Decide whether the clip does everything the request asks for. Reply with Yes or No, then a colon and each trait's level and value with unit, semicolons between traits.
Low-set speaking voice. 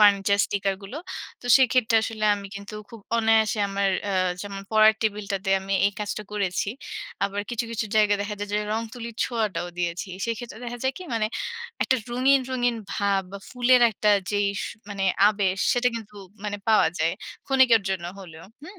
No: high, 215 Hz